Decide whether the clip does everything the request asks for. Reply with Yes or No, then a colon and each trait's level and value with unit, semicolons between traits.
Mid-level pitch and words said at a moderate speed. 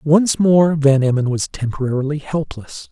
Yes: medium, 145 Hz; average, 145 wpm